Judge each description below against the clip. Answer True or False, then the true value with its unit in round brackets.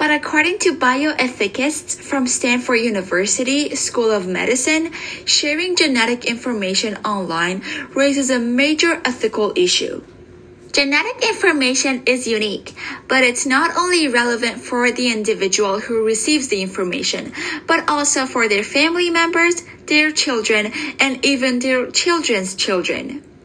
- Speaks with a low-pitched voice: False (260 Hz)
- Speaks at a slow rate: True (125 wpm)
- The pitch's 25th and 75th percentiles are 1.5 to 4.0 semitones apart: False (5.3 semitones)